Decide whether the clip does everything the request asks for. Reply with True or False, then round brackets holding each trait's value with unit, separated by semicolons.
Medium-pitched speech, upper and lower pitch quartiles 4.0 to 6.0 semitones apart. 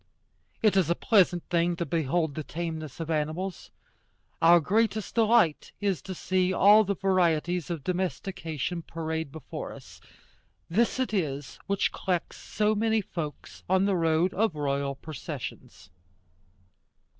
False (175 Hz; 3.5 semitones)